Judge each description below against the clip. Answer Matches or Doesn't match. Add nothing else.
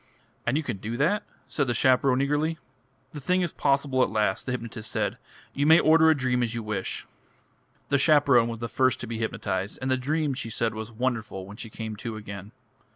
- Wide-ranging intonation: Doesn't match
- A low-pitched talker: Matches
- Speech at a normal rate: Doesn't match